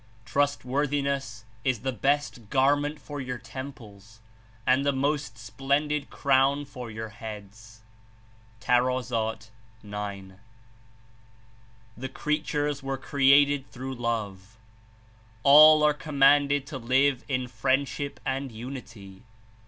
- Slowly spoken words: Yes, slow, 105 wpm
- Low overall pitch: Yes, low, 130 Hz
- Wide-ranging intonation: No, average, 4.0 semitones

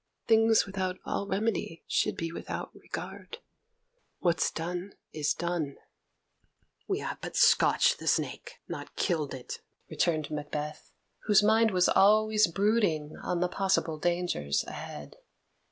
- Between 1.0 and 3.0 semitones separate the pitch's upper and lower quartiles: No, average, 5.0 semitones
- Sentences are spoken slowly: Yes, slow, 125 wpm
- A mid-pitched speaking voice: Yes, medium, 180 Hz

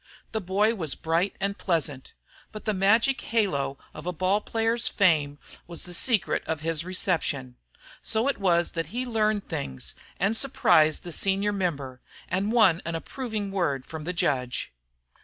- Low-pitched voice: No, medium, 185 Hz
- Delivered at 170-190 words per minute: No, average, 160 wpm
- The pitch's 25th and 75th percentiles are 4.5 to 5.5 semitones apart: Yes, average, 5.0 semitones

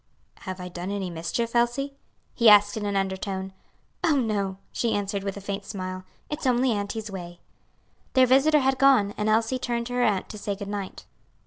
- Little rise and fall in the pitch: No, average, 3.9 semitones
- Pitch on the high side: Yes, high, 205 Hz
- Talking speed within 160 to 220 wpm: Yes, average, 195 wpm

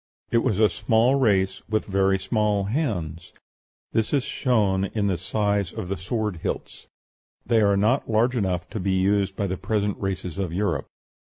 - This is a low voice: Yes, low, 100 Hz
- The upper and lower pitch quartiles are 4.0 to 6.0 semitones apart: No, narrow, 2.5 semitones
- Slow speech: No, average, 175 wpm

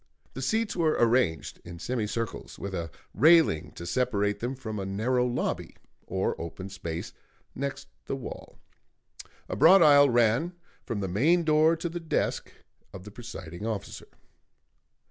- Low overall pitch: Yes, low, 120 Hz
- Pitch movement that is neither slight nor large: No, wide, 7.3 semitones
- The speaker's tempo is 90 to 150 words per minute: Yes, average, 145 wpm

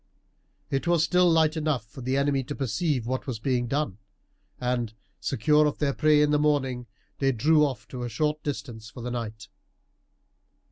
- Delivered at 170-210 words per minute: Yes, average, 180 wpm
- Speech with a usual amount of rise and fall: Yes, average, 3.7 semitones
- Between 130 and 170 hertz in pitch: Yes, low, 135 Hz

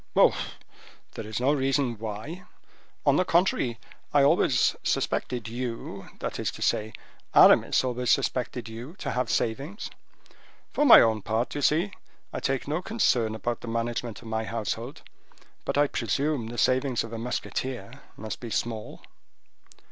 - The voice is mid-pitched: No, low, 120 Hz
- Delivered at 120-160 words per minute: Yes, average, 150 wpm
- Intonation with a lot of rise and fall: No, average, 3.6 semitones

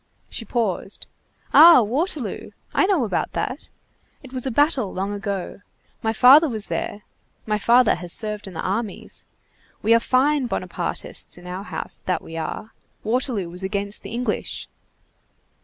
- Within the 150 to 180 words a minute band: Yes, average, 155 wpm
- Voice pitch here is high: Yes, high, 220 Hz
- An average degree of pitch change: Yes, average, 4.3 semitones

